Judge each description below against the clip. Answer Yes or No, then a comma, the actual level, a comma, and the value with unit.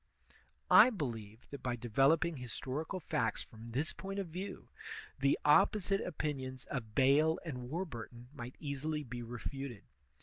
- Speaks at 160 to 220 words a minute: No, average, 140 wpm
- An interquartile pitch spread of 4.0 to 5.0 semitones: Yes, average, 4.7 semitones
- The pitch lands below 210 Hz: Yes, low, 135 Hz